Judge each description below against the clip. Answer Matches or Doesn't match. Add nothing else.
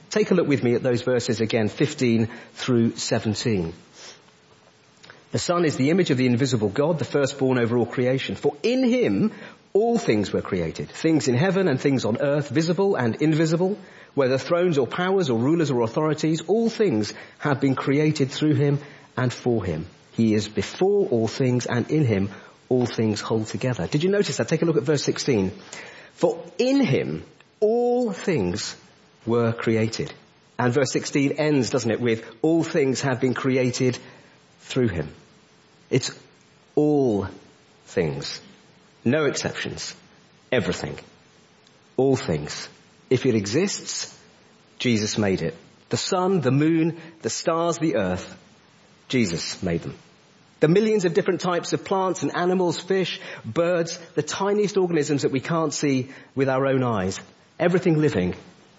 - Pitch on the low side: Doesn't match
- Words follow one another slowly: Doesn't match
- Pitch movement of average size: Doesn't match